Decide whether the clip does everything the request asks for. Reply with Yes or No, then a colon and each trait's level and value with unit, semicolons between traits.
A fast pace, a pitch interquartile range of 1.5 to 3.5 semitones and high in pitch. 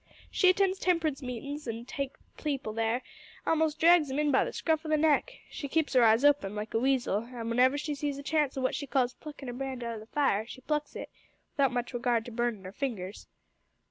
No: fast, 230 wpm; average, 4.0 semitones; very high, 270 Hz